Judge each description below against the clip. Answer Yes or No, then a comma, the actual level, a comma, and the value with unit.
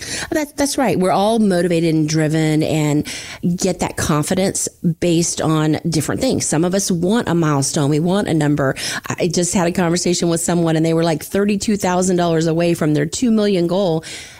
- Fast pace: No, average, 180 wpm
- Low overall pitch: No, medium, 170 Hz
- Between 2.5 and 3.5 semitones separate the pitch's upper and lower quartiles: Yes, average, 3.2 semitones